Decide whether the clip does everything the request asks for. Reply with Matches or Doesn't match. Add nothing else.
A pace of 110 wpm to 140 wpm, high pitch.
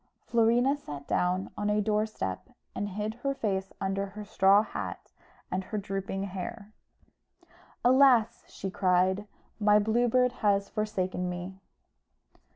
Matches